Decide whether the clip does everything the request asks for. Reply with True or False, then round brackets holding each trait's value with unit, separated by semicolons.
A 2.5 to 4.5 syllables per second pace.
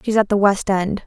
False (5.4 syllables/s)